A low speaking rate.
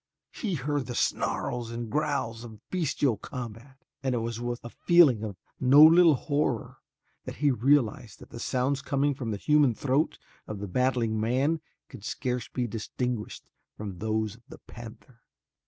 No: average, 165 wpm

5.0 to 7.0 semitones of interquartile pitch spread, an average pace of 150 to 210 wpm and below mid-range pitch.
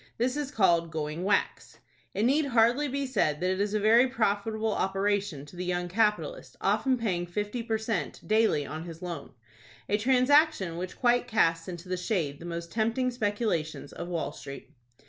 No: wide, 5.4 semitones; average, 175 wpm; high, 205 Hz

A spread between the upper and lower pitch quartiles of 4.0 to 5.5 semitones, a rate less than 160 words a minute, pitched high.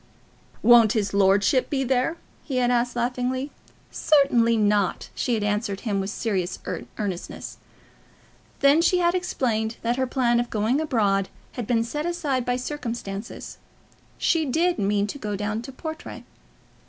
Yes: average, 4.5 semitones; average, 145 wpm; high, 240 Hz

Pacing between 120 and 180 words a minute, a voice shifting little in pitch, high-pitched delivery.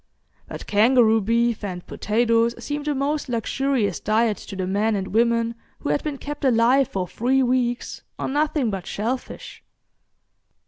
No: average, 150 wpm; average, 3.8 semitones; high, 235 Hz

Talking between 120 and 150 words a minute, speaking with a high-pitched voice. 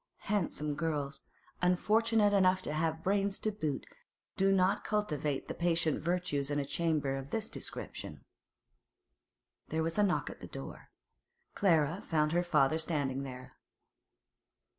No: slow, 135 wpm; medium, 165 Hz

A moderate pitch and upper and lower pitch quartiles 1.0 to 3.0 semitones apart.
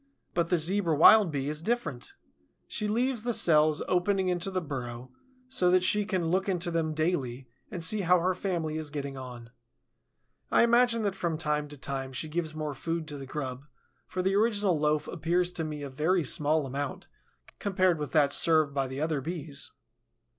No: medium, 160 Hz; average, 4.1 semitones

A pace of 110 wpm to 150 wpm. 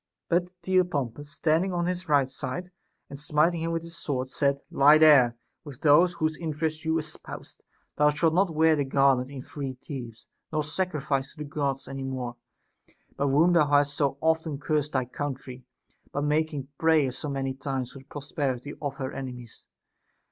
No: average, 175 wpm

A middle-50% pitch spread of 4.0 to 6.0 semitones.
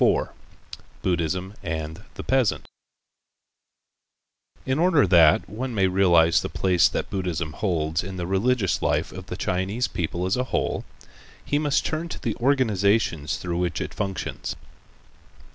Yes: average, 5.2 semitones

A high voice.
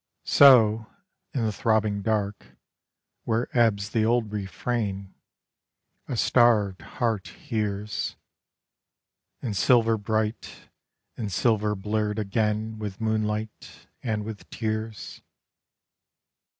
No: low, 110 Hz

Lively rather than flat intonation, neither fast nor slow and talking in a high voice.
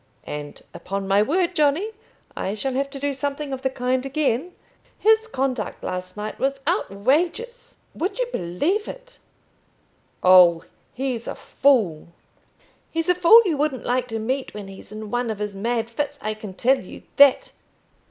Yes: wide, 6.4 semitones; average, 170 wpm; very high, 260 Hz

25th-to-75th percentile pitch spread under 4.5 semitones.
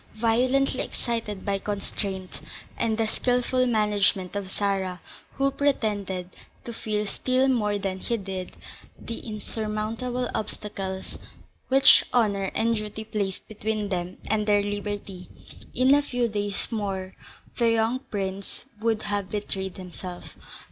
Yes: average, 2.9 semitones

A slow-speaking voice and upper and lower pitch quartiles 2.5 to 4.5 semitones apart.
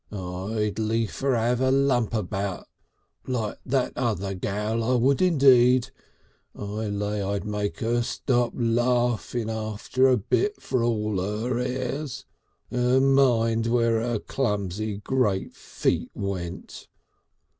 Yes: slow, 120 wpm; average, 3.2 semitones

